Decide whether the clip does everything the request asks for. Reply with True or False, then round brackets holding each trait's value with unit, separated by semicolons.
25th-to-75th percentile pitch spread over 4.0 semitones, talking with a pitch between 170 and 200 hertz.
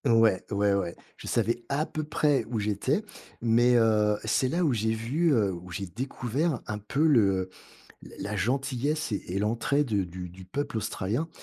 False (5.5 semitones; 115 Hz)